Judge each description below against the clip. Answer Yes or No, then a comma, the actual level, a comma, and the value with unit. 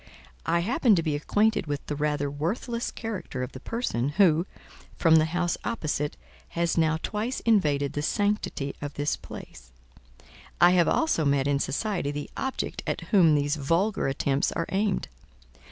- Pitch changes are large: Yes, wide, 5.9 semitones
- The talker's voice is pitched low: No, medium, 160 Hz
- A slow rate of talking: No, average, 160 wpm